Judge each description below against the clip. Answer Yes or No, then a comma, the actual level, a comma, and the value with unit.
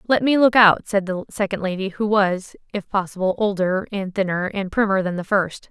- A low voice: No, high, 195 Hz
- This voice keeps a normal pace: No, fast, 210 wpm